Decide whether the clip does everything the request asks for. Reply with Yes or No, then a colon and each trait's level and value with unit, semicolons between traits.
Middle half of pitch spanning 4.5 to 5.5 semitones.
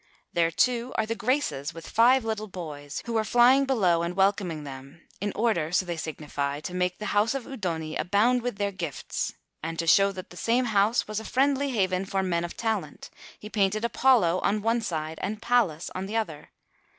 Yes: average, 5.2 semitones